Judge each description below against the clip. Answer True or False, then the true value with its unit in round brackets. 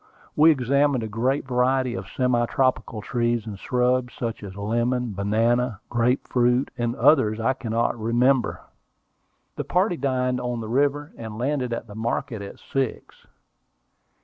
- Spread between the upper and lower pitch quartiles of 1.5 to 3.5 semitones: True (2.4 semitones)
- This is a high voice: False (125 Hz)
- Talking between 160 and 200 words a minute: False (150 wpm)